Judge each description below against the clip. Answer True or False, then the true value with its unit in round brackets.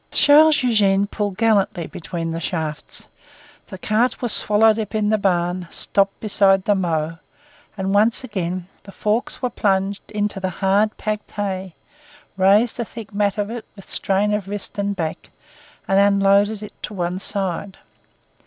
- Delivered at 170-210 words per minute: False (160 wpm)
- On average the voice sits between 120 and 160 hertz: False (200 Hz)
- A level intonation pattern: True (2.0 semitones)